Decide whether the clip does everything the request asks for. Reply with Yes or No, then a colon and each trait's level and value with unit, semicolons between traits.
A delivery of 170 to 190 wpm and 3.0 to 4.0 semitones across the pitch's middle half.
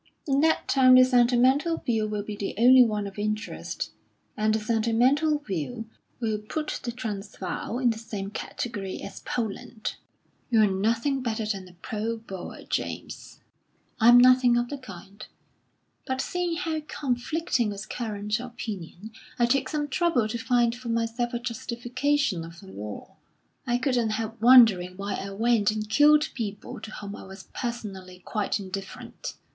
No: average, 155 wpm; average, 3.5 semitones